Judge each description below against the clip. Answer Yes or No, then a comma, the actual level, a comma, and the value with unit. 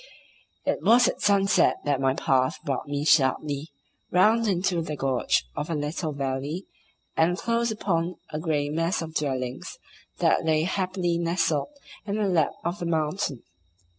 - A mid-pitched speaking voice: Yes, medium, 160 Hz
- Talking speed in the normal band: Yes, average, 155 wpm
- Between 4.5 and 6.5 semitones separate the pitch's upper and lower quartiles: No, average, 4.1 semitones